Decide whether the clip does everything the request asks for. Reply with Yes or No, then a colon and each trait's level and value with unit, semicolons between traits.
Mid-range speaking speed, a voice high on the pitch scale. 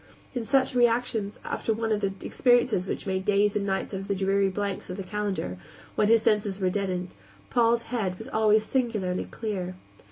Yes: average, 190 wpm; high, 205 Hz